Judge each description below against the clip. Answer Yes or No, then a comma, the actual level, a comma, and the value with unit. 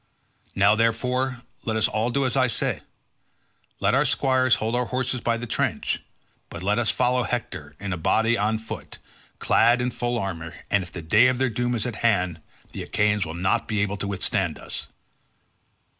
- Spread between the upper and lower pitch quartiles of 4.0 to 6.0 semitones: No, average, 3.5 semitones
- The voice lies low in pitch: Yes, low, 115 Hz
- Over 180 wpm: Yes, average, 190 wpm